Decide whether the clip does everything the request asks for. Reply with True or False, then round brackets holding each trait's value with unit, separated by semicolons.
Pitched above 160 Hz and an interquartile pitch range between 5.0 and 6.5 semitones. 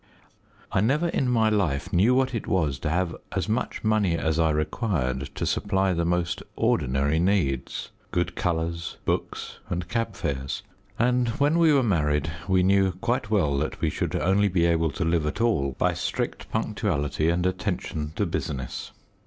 False (90 Hz; 5.4 semitones)